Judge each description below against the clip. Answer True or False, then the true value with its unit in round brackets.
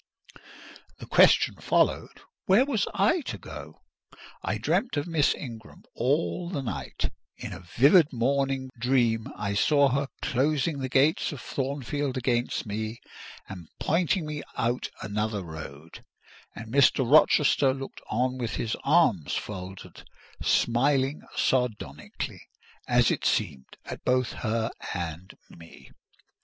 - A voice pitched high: False (130 Hz)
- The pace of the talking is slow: True (125 wpm)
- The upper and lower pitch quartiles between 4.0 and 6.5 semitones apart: True (4.6 semitones)